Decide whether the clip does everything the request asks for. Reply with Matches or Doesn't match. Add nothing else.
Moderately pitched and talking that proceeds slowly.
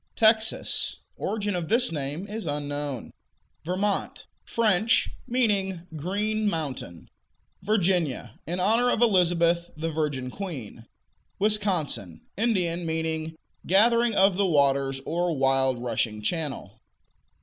Matches